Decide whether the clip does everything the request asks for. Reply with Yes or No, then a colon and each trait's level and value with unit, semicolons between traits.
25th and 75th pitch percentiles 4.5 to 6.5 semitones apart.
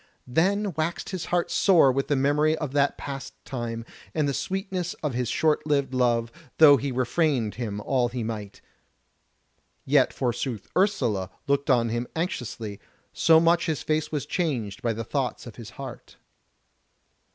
Yes: average, 4.9 semitones